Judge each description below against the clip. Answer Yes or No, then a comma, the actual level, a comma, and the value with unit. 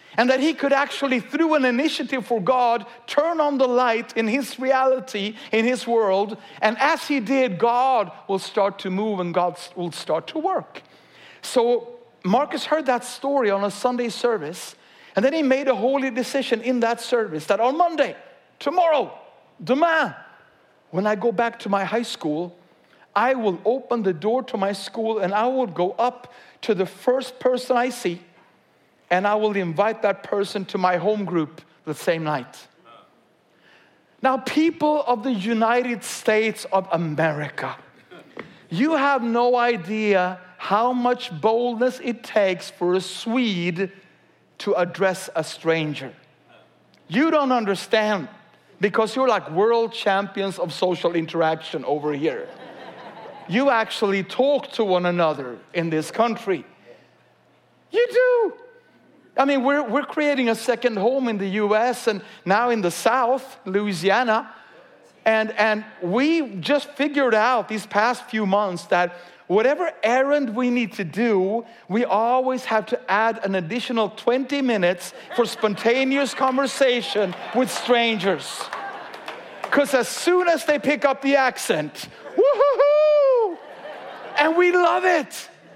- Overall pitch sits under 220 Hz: No, high, 230 Hz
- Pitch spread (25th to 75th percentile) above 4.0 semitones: Yes, average, 5.2 semitones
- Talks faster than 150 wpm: No, average, 145 wpm